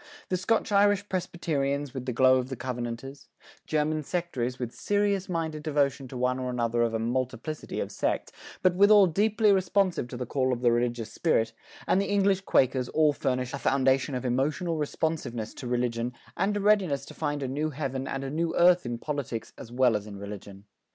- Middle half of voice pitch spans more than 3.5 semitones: Yes, wide, 5.6 semitones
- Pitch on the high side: No, low, 135 Hz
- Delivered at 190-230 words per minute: Yes, average, 195 wpm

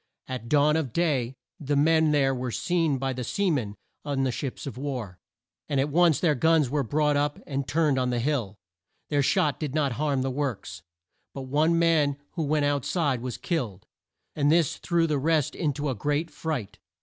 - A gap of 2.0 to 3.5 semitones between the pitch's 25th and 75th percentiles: Yes, average, 3.1 semitones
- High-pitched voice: No, medium, 145 Hz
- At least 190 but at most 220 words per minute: Yes, average, 200 wpm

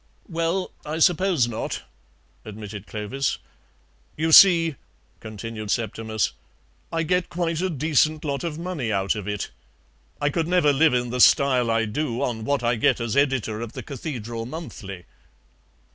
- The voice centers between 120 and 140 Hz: Yes, low, 135 Hz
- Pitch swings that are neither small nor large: No, wide, 6.4 semitones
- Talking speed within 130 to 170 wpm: Yes, average, 150 wpm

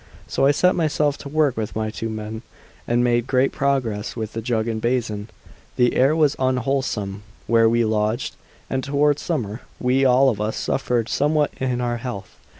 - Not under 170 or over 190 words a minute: Yes, average, 180 wpm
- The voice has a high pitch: No, low, 125 Hz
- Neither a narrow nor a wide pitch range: Yes, average, 3.7 semitones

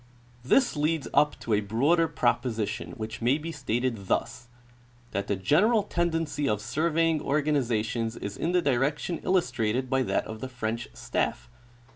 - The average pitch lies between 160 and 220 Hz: No, low, 130 Hz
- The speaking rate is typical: Yes, average, 155 wpm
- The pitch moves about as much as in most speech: No, wide, 5.9 semitones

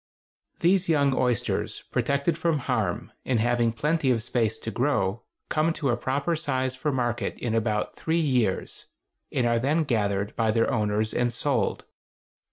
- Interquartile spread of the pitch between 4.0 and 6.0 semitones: Yes, average, 4.4 semitones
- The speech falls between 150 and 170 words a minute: Yes, average, 160 wpm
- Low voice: Yes, low, 125 Hz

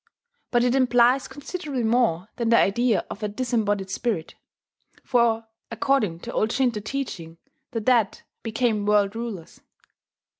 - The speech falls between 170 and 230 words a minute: No, slow, 135 wpm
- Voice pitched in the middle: No, high, 230 Hz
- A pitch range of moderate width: Yes, average, 3.2 semitones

